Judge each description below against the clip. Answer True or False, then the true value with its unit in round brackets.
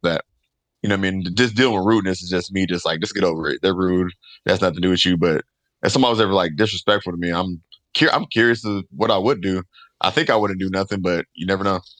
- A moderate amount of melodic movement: False (2.3 semitones)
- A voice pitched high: False (95 Hz)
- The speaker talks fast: True (275 wpm)